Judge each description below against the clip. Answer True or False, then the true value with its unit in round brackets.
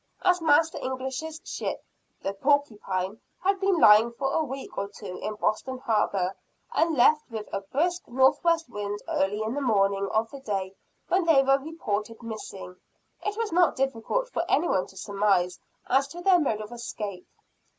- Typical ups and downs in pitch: False (7.3 semitones)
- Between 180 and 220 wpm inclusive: False (170 wpm)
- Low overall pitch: False (245 Hz)